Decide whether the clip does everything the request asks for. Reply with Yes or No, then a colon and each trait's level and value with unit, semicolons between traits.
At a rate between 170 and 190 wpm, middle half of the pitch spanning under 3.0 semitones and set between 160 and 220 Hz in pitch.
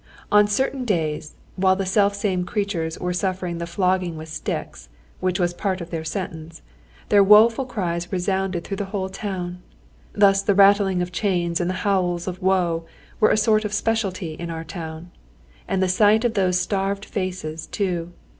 Yes: average, 175 wpm; narrow, 2.6 semitones; medium, 185 Hz